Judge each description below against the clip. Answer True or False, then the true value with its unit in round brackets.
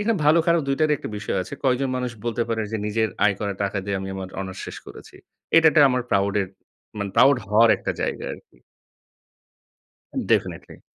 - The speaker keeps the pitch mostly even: False (5.4 semitones)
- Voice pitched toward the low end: True (115 Hz)